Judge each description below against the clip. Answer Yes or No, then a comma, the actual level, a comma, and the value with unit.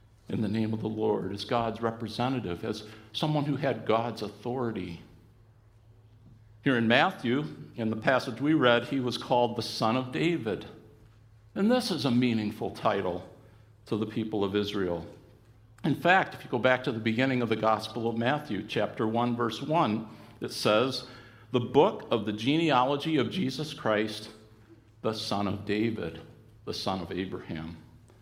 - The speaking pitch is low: Yes, low, 110 Hz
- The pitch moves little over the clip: Yes, narrow, 2.2 semitones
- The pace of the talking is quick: No, average, 165 wpm